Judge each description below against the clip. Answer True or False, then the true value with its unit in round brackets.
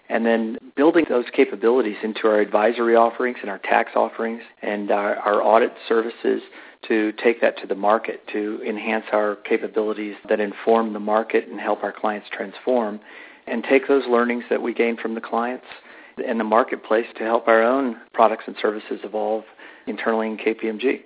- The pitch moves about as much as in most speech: False (1.5 semitones)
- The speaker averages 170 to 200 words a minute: True (175 wpm)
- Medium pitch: False (115 Hz)